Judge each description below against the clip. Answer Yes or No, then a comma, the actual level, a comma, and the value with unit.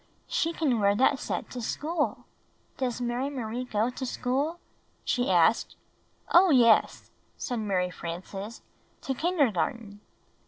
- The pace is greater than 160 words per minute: No, average, 140 wpm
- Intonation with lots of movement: No, average, 4.8 semitones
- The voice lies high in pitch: Yes, high, 245 Hz